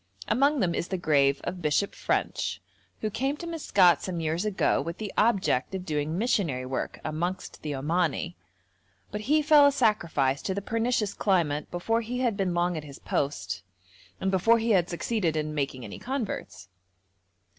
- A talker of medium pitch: Yes, medium, 180 Hz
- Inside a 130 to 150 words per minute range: No, average, 175 wpm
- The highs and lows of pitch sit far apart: Yes, wide, 6.5 semitones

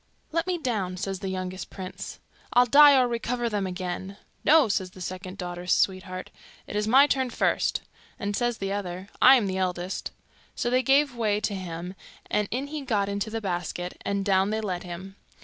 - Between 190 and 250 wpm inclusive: Yes, average, 195 wpm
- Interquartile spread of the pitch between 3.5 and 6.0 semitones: Yes, average, 4.6 semitones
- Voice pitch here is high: Yes, high, 200 Hz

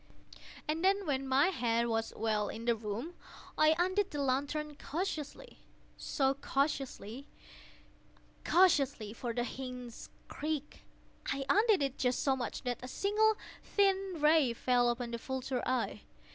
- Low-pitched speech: No, very high, 270 Hz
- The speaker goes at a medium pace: No, slow, 130 wpm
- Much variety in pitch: No, average, 4.9 semitones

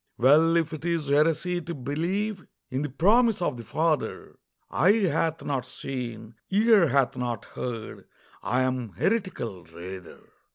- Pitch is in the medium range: Yes, medium, 150 Hz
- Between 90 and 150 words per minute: Yes, average, 140 wpm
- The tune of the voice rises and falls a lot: Yes, wide, 6.0 semitones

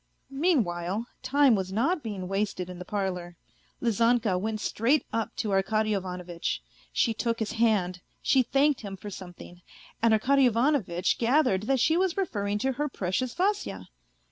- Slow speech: No, average, 160 wpm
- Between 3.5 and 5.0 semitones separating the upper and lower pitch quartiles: No, wide, 5.6 semitones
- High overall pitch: Yes, high, 220 Hz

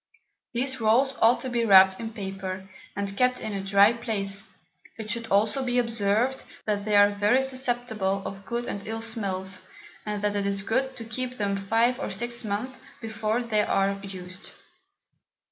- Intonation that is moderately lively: Yes, average, 3.2 semitones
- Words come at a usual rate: Yes, average, 175 wpm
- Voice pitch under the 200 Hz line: No, high, 215 Hz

